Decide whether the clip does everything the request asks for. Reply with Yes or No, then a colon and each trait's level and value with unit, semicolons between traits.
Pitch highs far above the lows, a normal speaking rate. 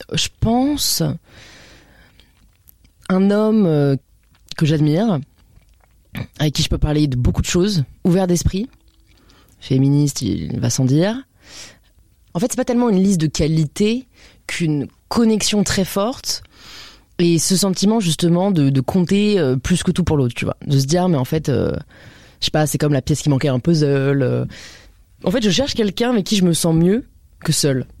Yes: wide, 7.8 semitones; average, 170 wpm